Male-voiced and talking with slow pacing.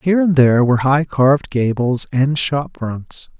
No: male; average, 175 wpm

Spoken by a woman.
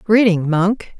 Yes: female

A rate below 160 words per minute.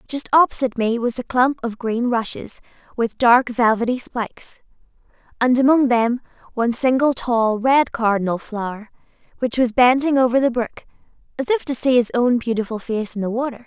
No: average, 170 wpm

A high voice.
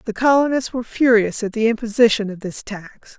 Yes: high, 225 Hz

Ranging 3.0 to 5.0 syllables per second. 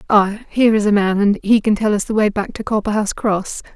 No: 6.2 syllables/s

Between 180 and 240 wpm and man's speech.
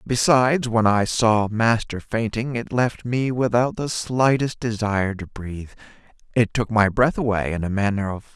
No: average, 170 wpm; male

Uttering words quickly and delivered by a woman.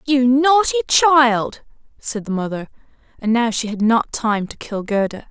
No: average, 170 wpm; female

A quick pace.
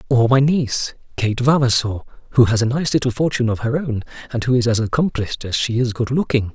Yes: fast, 220 wpm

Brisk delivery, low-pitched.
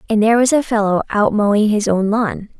No: fast, 230 wpm; high, 215 Hz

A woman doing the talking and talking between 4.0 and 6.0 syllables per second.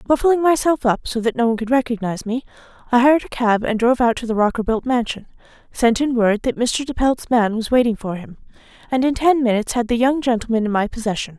No: female; 6.4 syllables/s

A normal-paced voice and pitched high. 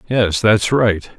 No: average, 150 wpm; low, 105 Hz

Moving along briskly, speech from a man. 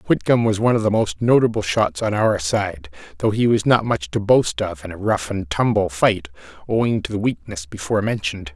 Yes: fast, 215 wpm; male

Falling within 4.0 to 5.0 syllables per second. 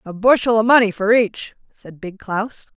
Yes: 4.5 syllables/s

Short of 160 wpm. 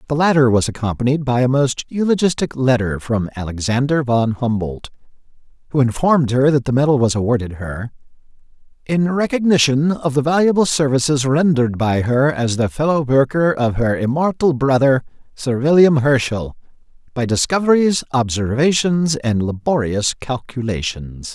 Yes: slow, 135 wpm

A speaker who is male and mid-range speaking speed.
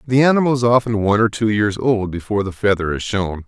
No: male; fast, 240 wpm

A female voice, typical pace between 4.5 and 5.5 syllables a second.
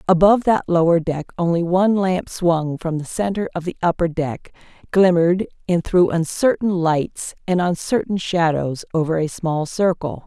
Yes: female; 4.8 syllables/s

